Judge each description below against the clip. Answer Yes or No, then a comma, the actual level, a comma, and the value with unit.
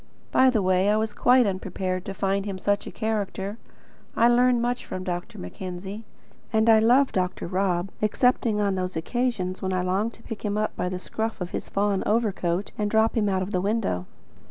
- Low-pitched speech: No, high, 200 Hz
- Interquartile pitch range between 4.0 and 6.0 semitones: No, average, 3.2 semitones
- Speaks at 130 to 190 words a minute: No, fast, 205 wpm